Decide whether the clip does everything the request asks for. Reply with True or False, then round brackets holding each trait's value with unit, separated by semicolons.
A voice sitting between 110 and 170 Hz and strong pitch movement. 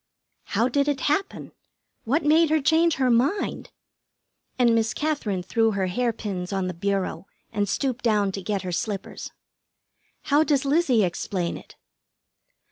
False (230 Hz; 6.4 semitones)